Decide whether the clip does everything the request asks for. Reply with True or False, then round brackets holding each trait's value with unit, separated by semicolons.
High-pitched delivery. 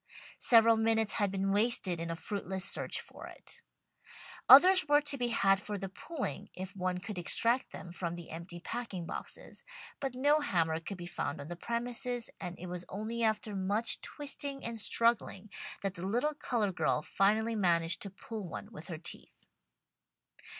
True (205 Hz)